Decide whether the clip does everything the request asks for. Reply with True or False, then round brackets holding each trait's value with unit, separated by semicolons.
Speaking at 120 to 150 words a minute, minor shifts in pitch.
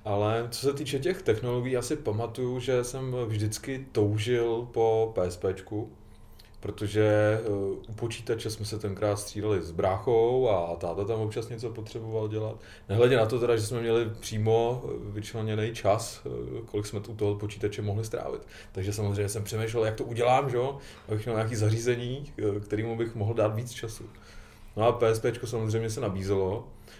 False (160 wpm; 2.0 semitones)